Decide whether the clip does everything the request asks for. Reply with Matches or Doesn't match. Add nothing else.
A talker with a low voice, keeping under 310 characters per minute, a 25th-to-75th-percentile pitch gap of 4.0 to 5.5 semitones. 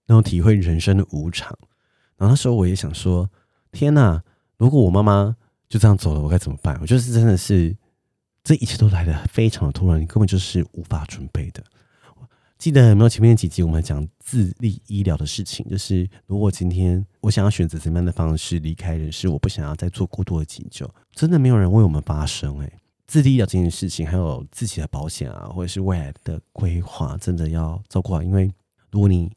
Doesn't match